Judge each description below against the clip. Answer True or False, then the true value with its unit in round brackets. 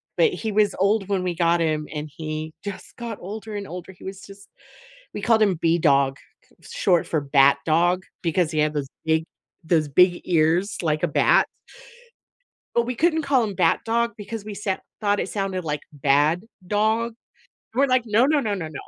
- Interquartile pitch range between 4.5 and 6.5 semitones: True (5.2 semitones)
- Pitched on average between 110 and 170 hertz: False (185 Hz)